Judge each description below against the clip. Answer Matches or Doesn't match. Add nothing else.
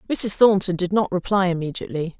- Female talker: Matches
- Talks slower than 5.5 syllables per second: Doesn't match